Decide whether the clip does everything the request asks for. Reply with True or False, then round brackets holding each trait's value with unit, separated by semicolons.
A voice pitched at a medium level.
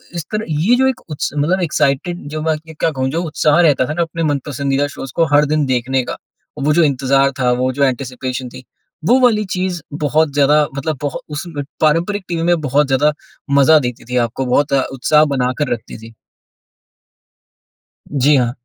True (145 Hz)